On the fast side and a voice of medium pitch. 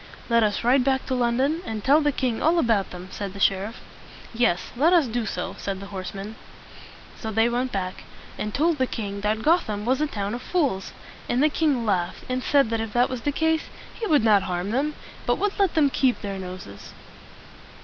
No: fast, 210 wpm; high, 235 Hz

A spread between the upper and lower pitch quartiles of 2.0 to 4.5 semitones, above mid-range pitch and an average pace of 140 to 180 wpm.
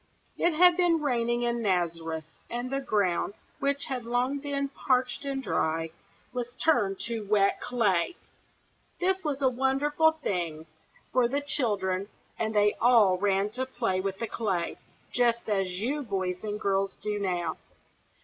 No: wide, 5.6 semitones; high, 230 Hz; average, 150 wpm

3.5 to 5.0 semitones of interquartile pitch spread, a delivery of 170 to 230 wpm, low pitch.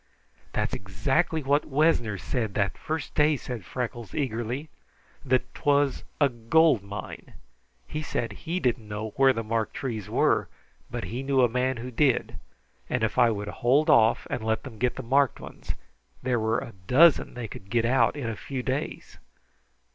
Yes: average, 3.8 semitones; average, 175 wpm; low, 125 Hz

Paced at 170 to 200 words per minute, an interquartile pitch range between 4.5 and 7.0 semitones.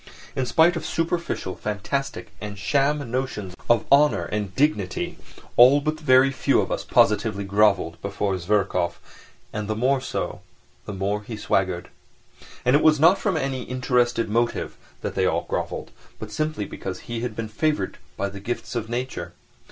No: average, 160 wpm; average, 5.2 semitones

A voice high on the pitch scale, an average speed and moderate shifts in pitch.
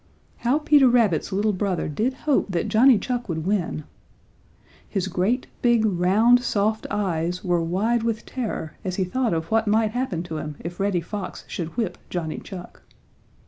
Yes: high, 205 Hz; average, 170 wpm; average, 4.9 semitones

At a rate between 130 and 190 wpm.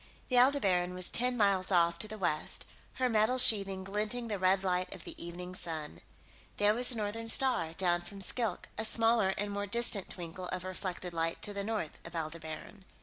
No: average, 200 wpm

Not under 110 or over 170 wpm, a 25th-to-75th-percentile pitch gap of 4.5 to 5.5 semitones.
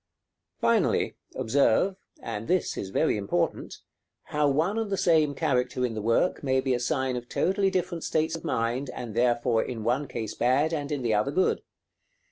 No: average, 180 wpm; average, 5.1 semitones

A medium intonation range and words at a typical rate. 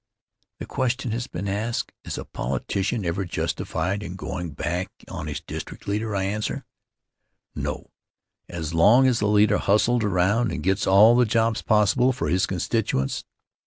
Yes: average, 3.7 semitones; average, 160 wpm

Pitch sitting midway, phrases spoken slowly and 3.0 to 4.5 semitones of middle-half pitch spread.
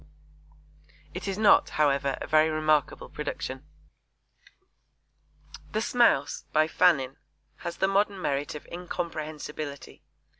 Yes: medium, 155 Hz; slow, 105 wpm; average, 3.7 semitones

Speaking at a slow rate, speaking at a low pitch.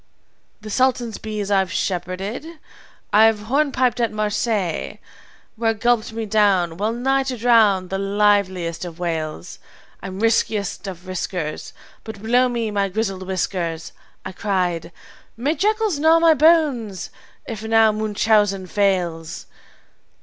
No: slow, 120 wpm; high, 210 Hz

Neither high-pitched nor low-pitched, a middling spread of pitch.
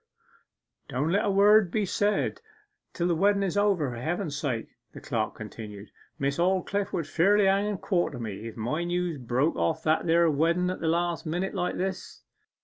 Yes: medium, 170 Hz; average, 5.0 semitones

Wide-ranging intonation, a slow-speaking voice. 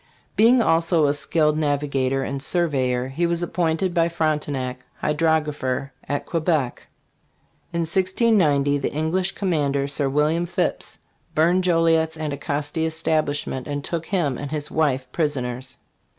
No: average, 2.9 semitones; slow, 125 wpm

